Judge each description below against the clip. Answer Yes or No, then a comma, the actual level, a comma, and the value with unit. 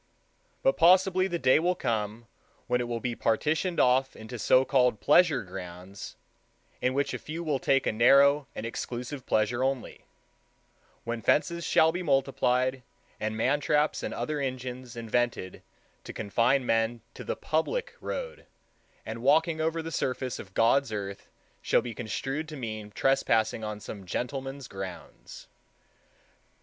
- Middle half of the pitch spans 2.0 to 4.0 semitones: No, average, 4.7 semitones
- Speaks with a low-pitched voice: Yes, low, 130 Hz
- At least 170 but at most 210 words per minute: No, average, 145 wpm